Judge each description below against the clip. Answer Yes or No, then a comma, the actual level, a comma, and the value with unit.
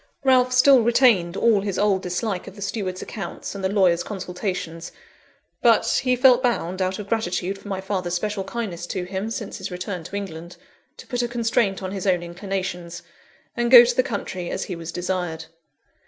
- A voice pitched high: Yes, high, 195 Hz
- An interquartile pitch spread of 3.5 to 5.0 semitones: Yes, average, 4.2 semitones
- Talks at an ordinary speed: Yes, average, 190 wpm